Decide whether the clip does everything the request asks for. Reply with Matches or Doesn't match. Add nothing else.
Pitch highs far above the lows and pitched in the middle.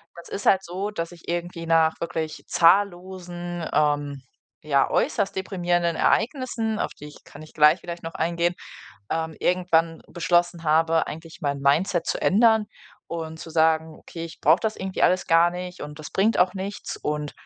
Doesn't match